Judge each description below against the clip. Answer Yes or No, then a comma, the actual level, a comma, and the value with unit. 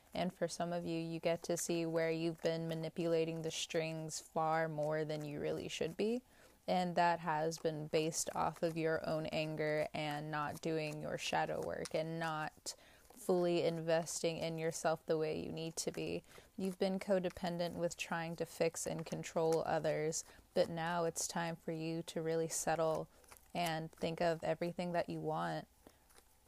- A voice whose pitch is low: No, medium, 165 Hz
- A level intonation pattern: Yes, narrow, 1.2 semitones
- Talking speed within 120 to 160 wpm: No, average, 170 wpm